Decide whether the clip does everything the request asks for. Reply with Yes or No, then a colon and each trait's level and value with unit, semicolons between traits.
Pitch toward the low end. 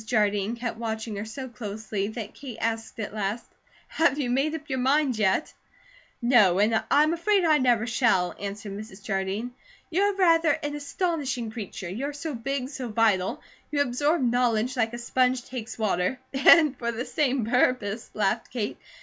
No: high, 240 Hz